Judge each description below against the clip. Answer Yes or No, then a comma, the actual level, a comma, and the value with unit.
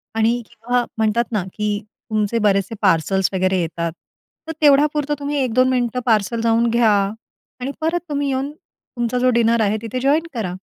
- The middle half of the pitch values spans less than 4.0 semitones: Yes, average, 3.5 semitones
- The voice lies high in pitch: Yes, high, 230 Hz